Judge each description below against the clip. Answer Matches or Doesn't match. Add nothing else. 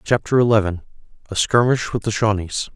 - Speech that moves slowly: Matches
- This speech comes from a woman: Doesn't match